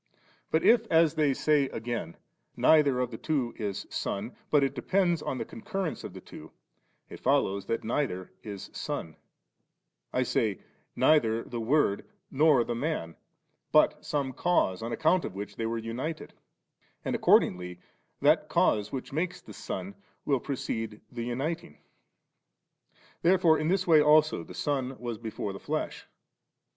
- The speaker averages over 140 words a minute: Yes, average, 155 wpm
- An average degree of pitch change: No, wide, 5.8 semitones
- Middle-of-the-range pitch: No, low, 130 Hz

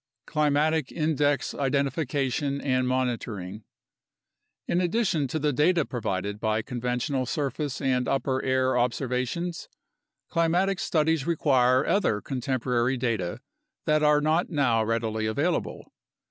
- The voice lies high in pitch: No, low, 135 Hz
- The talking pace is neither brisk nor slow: No, slow, 110 wpm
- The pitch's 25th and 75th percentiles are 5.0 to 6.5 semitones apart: No, average, 3.8 semitones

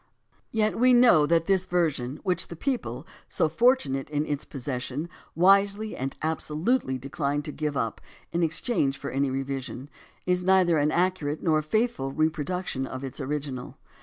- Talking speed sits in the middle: Yes, average, 165 wpm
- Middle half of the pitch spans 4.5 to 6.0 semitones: Yes, average, 5.2 semitones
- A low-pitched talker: No, medium, 155 Hz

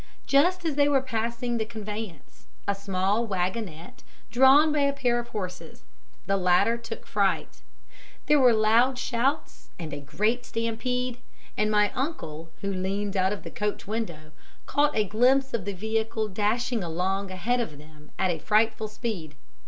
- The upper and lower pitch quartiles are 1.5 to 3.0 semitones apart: No, average, 4.3 semitones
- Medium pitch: No, high, 220 Hz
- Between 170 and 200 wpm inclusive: No, average, 160 wpm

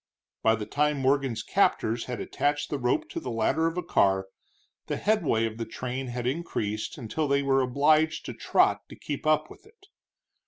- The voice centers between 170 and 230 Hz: No, low, 135 Hz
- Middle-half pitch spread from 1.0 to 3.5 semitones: No, average, 5.0 semitones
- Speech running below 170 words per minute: No, average, 190 wpm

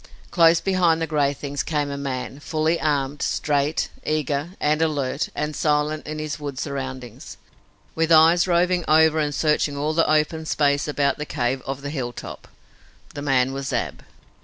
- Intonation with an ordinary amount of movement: No, narrow, 2.1 semitones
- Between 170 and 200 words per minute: No, average, 160 wpm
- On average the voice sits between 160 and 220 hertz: No, medium, 150 Hz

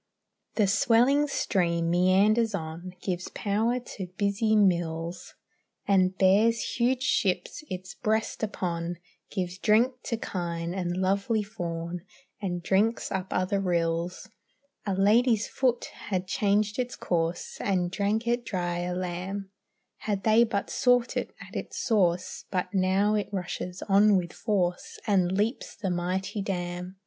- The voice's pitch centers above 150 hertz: Yes, high, 190 Hz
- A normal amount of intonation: Yes, average, 3.2 semitones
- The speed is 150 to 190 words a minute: No, slow, 135 wpm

